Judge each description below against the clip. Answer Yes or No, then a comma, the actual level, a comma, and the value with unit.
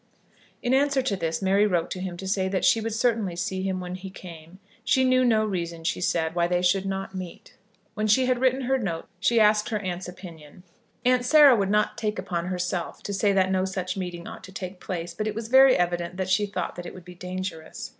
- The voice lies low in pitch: No, high, 190 Hz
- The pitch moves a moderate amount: Yes, average, 3.3 semitones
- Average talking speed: No, fast, 235 wpm